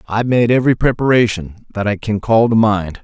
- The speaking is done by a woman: No, male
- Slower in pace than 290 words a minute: Yes, average, 200 wpm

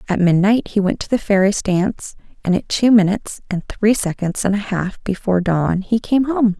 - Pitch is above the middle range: Yes, high, 200 Hz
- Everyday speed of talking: No, fast, 210 wpm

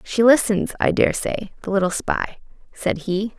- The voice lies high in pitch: Yes, high, 205 Hz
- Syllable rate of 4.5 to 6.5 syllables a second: No, 4.3 syllables/s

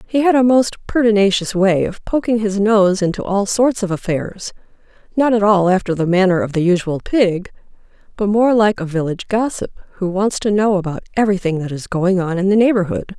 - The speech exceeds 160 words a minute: Yes, average, 200 wpm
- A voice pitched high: Yes, high, 200 Hz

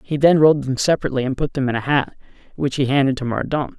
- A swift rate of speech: Yes, fast, 255 wpm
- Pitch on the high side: No, low, 135 Hz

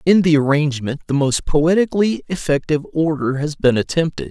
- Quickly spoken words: No, average, 155 wpm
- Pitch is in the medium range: Yes, medium, 155 Hz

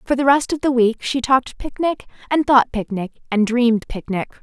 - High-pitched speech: Yes, very high, 250 Hz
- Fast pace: Yes, fast, 215 wpm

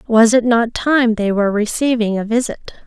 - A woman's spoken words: Yes, female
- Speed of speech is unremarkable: Yes, average, 190 wpm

